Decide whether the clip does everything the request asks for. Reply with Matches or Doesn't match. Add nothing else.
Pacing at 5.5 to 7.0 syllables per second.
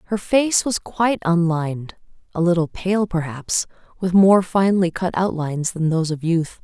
Doesn't match